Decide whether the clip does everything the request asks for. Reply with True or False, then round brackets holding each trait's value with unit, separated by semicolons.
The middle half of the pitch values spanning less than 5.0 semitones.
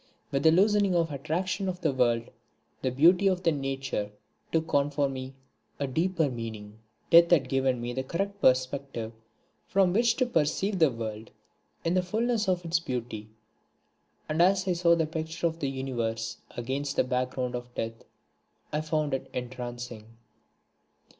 False (5.6 semitones)